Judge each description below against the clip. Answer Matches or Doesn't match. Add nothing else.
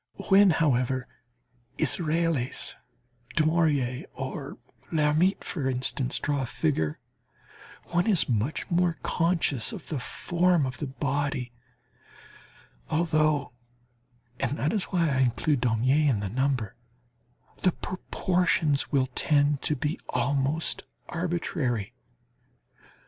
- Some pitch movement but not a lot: Matches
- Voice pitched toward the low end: Doesn't match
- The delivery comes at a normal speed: Doesn't match